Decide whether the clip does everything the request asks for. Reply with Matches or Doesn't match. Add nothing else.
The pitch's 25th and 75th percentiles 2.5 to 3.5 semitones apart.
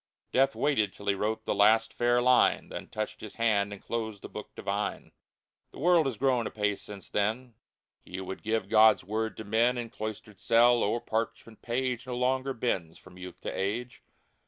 Matches